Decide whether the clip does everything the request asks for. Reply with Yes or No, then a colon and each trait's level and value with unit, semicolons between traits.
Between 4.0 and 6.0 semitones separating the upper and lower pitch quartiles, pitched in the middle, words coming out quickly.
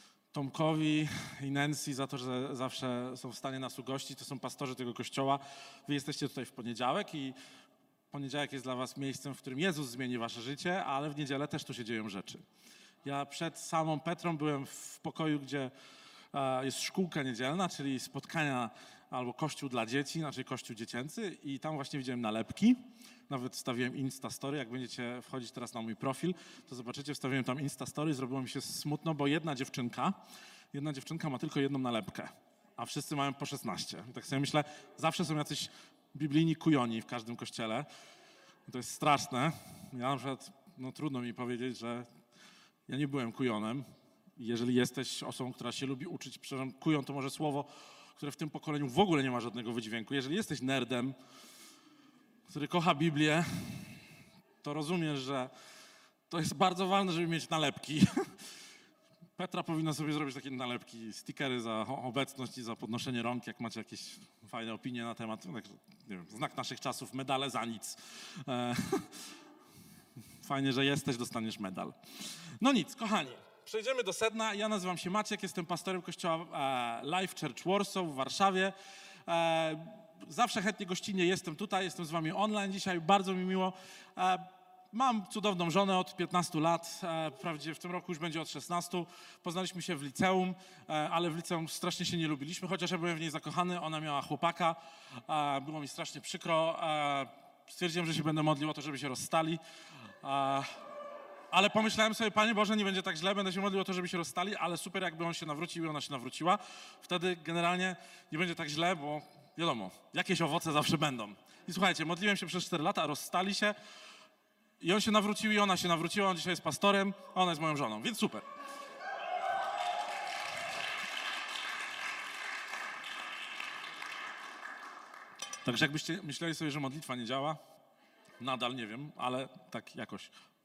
Yes: average, 5.3 semitones; medium, 155 Hz; fast, 165 wpm